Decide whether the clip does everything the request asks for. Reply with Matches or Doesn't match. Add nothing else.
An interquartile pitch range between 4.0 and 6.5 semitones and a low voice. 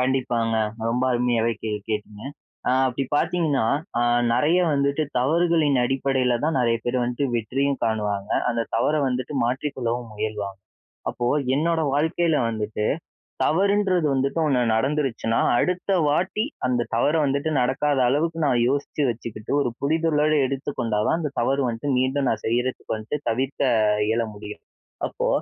Matches